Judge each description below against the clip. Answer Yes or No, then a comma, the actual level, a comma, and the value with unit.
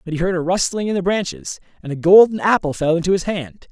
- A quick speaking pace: Yes, fast, 260 wpm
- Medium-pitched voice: Yes, medium, 175 Hz